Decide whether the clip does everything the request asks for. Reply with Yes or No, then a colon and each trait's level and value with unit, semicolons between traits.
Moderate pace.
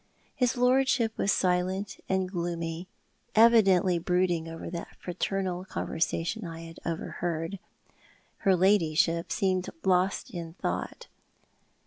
No: slow, 105 wpm